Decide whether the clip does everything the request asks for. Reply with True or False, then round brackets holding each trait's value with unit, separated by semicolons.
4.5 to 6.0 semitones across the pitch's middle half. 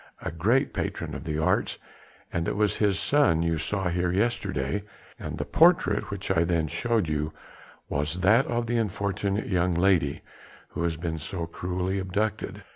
False (3.9 semitones)